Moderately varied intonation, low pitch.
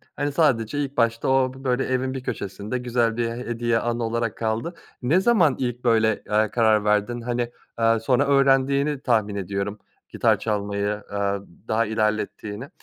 Yes: average, 3.3 semitones; low, 115 Hz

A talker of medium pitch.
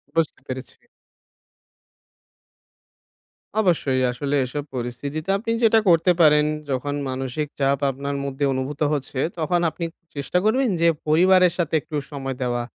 Yes: medium, 145 Hz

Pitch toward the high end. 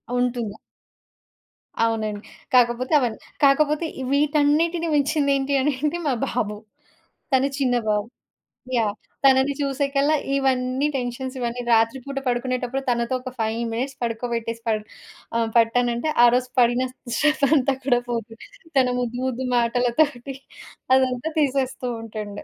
Yes: very high, 250 Hz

